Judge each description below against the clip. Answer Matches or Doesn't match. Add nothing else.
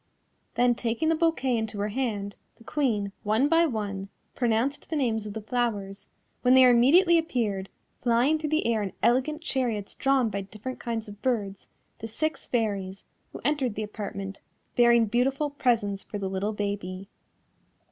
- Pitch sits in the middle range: Doesn't match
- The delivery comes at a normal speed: Matches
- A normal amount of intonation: Matches